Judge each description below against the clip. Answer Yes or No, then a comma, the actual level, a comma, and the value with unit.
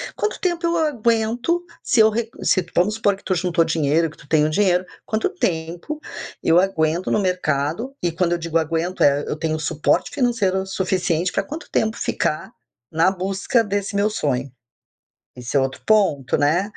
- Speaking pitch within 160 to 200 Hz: Yes, medium, 185 Hz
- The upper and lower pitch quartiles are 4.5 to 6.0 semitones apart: Yes, average, 5.2 semitones